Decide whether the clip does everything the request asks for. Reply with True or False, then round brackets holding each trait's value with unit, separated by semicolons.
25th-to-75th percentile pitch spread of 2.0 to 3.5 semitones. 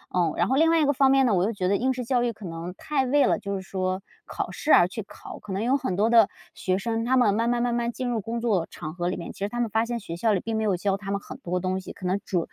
False (4.4 semitones)